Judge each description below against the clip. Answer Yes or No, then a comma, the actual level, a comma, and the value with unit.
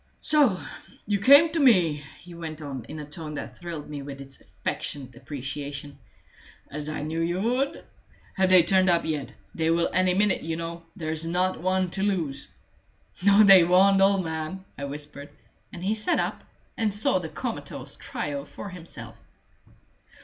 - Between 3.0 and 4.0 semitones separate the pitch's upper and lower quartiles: No, average, 4.4 semitones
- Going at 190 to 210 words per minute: No, average, 170 wpm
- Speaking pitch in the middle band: Yes, medium, 170 Hz